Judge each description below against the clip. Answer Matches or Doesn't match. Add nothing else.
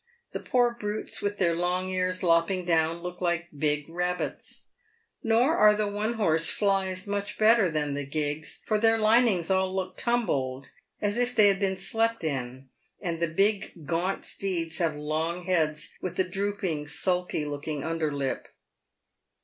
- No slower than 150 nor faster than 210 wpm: Matches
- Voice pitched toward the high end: Doesn't match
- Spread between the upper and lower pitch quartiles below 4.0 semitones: Doesn't match